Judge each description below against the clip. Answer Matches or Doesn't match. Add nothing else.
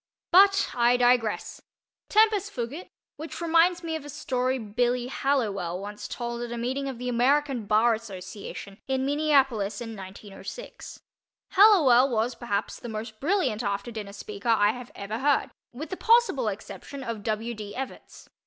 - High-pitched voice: Matches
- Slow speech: Doesn't match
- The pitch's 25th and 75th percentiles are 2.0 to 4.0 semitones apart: Doesn't match